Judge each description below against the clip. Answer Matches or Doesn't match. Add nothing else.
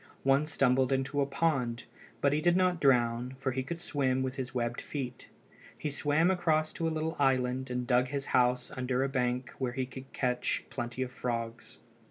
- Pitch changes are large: Doesn't match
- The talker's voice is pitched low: Matches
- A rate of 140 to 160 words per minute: Doesn't match